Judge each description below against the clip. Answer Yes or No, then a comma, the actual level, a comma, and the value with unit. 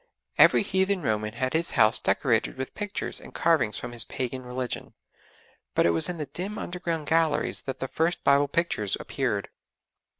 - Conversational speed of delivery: Yes, average, 170 wpm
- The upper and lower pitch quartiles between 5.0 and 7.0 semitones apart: Yes, wide, 5.6 semitones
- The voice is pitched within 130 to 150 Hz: Yes, medium, 140 Hz